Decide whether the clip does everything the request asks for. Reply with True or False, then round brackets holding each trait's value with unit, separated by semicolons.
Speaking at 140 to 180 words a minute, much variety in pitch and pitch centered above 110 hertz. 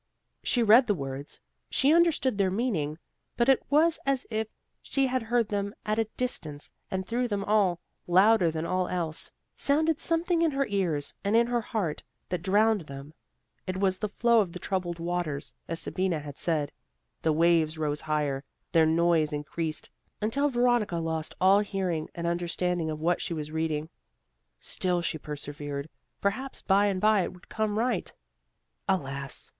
True (165 wpm; 5.8 semitones; 185 Hz)